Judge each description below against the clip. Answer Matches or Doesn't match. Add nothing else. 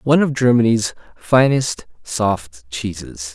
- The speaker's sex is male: Matches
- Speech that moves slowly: Matches